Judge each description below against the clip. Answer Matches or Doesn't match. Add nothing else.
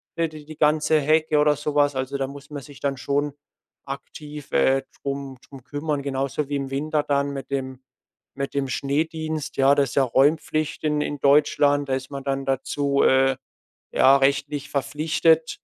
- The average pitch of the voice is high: Doesn't match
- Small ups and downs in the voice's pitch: Matches